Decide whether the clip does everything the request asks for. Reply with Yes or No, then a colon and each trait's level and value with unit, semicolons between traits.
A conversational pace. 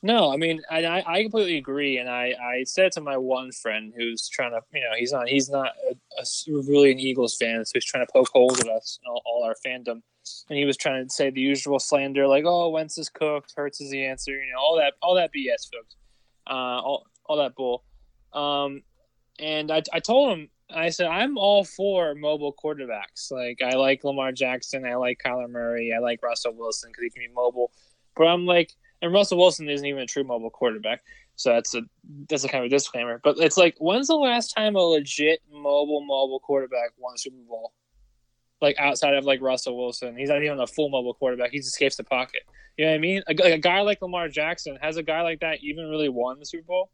No: fast, 235 wpm